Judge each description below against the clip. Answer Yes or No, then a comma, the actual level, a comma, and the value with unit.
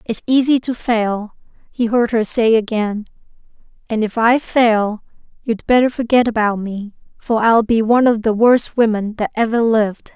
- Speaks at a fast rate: No, average, 170 wpm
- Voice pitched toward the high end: Yes, high, 225 Hz